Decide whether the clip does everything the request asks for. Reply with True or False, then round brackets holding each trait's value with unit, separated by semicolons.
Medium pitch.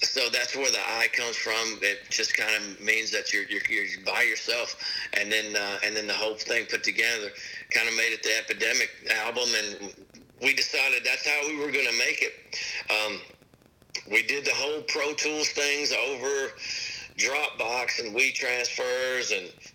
True (145 Hz)